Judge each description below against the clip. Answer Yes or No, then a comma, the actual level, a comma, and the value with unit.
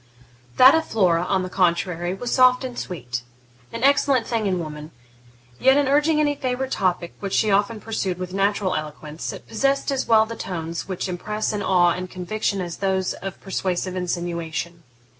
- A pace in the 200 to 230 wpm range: No, average, 175 wpm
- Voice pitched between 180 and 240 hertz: Yes, high, 190 Hz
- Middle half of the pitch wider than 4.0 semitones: Yes, average, 4.7 semitones